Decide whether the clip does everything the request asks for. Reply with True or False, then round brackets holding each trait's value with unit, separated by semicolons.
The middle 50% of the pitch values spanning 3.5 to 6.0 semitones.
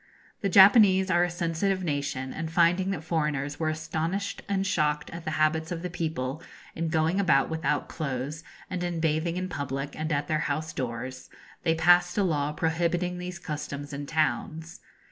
False (3.0 semitones)